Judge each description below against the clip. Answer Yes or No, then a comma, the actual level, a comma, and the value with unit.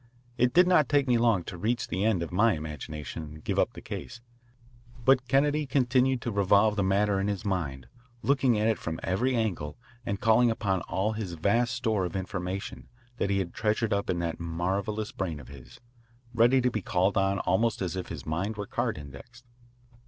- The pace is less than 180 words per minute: No, average, 200 wpm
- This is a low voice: Yes, low, 100 Hz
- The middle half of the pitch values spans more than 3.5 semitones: Yes, average, 5.0 semitones